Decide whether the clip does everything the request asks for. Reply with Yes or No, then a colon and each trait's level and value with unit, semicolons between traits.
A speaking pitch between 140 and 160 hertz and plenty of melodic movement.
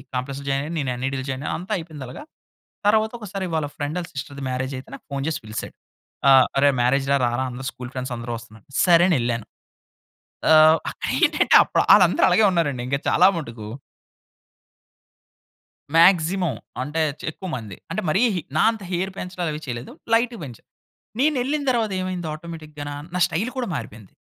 Yes: medium, 150 Hz; wide, 5.8 semitones